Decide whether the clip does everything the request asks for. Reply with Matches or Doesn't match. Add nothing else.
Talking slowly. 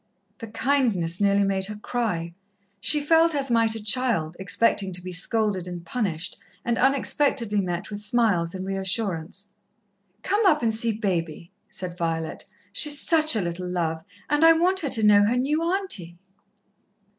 Doesn't match